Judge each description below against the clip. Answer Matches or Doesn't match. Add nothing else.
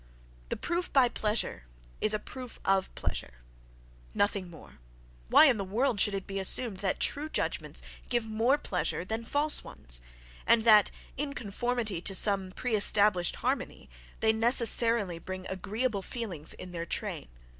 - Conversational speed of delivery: Matches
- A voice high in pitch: Matches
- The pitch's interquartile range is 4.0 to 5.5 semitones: Matches